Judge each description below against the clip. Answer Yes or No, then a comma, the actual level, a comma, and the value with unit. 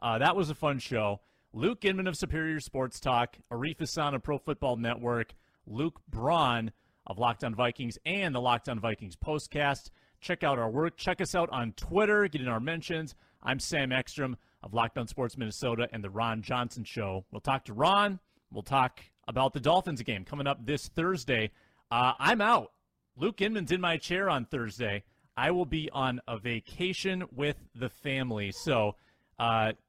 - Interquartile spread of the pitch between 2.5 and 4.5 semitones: No, wide, 5.4 semitones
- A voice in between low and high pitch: No, low, 130 Hz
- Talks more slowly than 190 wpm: Yes, average, 175 wpm